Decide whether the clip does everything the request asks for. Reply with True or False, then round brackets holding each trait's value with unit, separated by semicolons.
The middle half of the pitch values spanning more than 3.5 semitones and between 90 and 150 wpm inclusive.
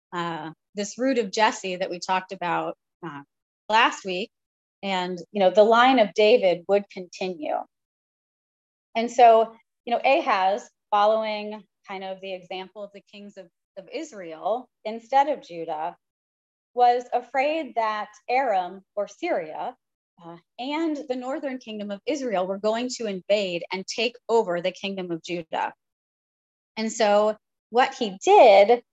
True (4.3 semitones; 145 wpm)